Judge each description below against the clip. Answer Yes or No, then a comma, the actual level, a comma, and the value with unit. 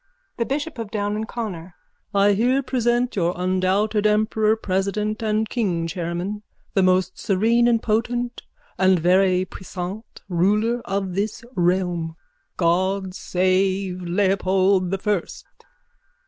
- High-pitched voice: Yes, high, 195 Hz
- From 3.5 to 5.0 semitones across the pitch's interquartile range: No, average, 2.9 semitones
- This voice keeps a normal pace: No, slow, 125 wpm